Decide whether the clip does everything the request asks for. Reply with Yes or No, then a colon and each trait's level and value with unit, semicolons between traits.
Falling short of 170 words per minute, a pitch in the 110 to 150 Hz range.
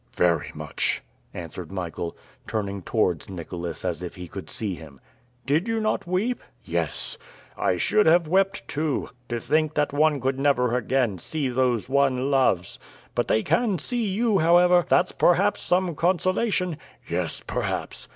Yes: average, 150 wpm; medium, 140 Hz